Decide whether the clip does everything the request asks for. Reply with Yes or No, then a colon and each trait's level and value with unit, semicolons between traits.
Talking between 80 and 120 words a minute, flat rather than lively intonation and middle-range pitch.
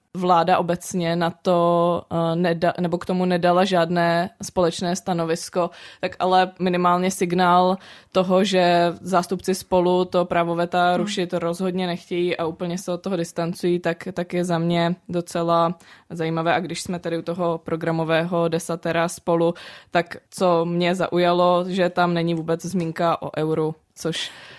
No: average, 140 wpm; narrow, 1.2 semitones; medium, 175 Hz